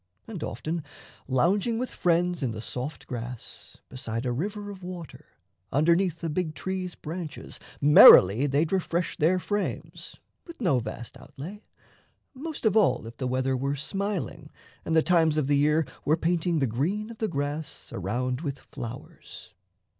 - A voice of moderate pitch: Yes, medium, 160 Hz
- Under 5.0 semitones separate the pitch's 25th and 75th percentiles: No, wide, 5.6 semitones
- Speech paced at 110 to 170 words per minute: Yes, average, 155 wpm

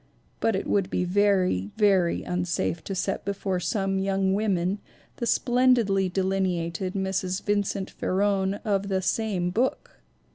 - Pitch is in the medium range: No, high, 195 Hz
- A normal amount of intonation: No, narrow, 1.7 semitones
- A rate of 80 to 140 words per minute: Yes, slow, 135 wpm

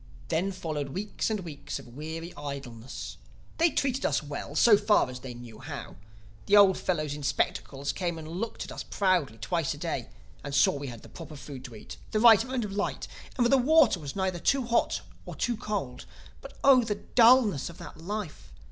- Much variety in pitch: Yes, wide, 7.1 semitones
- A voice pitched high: No, medium, 170 Hz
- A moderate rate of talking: No, fast, 210 wpm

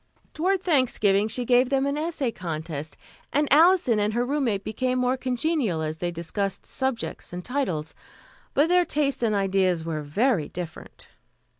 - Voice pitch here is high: Yes, high, 235 Hz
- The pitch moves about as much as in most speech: No, wide, 7.7 semitones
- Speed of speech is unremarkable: Yes, average, 155 wpm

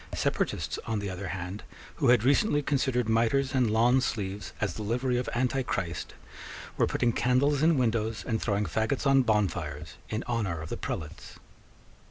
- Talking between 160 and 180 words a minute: Yes, average, 165 wpm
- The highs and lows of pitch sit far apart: No, average, 4.2 semitones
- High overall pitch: No, low, 115 Hz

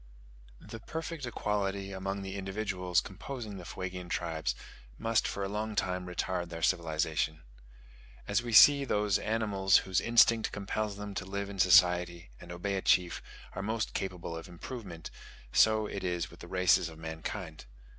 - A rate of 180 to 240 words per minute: No, average, 160 wpm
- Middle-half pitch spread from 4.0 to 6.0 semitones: No, average, 3.1 semitones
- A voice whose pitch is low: Yes, very low, 95 Hz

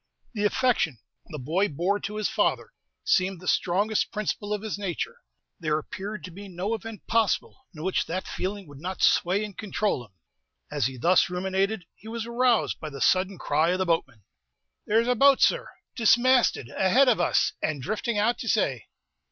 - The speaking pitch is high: Yes, high, 195 Hz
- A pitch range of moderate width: Yes, average, 4.2 semitones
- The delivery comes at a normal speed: Yes, average, 185 wpm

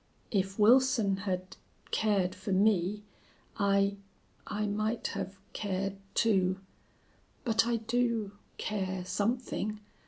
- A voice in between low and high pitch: No, high, 205 Hz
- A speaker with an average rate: No, slow, 100 wpm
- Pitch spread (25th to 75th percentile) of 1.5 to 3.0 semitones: Yes, narrow, 2.5 semitones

